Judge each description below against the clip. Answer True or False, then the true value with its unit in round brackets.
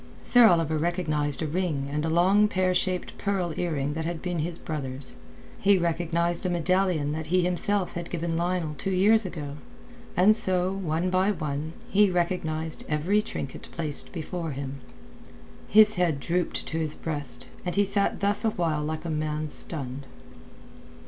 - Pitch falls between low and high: True (170 Hz)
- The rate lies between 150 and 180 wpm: True (160 wpm)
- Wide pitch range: False (3.1 semitones)